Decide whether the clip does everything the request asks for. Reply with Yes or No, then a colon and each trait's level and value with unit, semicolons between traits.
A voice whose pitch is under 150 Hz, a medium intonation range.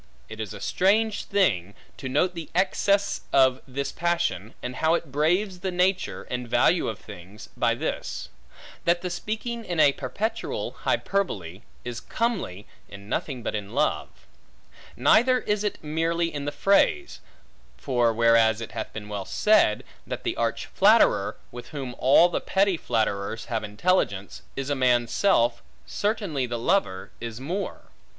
No: medium, 140 Hz; wide, 8.4 semitones